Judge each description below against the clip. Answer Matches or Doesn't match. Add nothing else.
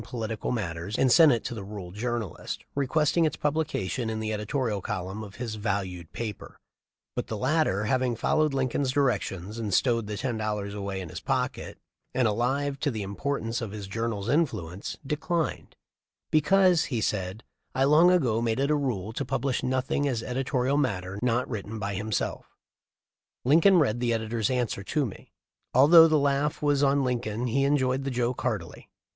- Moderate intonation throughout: Matches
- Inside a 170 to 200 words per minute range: Matches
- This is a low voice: Matches